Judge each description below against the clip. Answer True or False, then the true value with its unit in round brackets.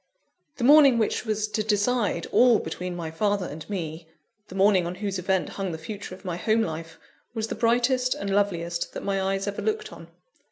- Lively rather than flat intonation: False (3.8 semitones)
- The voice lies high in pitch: True (200 Hz)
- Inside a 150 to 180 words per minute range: False (200 wpm)